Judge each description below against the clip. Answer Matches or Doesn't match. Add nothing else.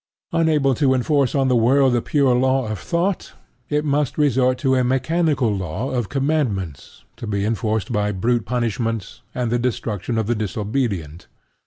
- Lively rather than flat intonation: Doesn't match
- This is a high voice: Doesn't match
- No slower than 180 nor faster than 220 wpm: Doesn't match